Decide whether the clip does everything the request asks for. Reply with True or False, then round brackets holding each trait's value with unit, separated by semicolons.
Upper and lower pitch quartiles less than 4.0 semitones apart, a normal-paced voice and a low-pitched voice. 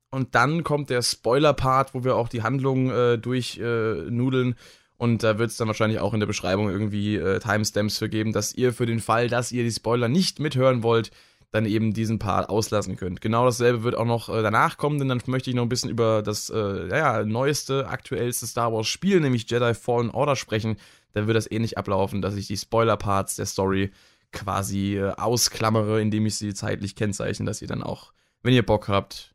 False (2.8 semitones; 210 wpm; 110 Hz)